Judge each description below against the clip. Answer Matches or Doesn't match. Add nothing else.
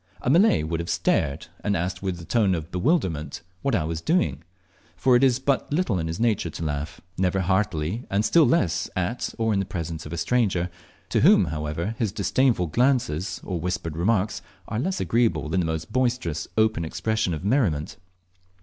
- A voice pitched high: Doesn't match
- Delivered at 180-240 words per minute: Matches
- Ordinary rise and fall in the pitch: Doesn't match